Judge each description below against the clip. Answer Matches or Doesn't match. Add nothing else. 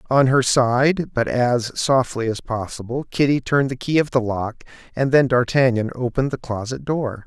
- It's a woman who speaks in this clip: Doesn't match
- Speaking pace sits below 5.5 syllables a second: Matches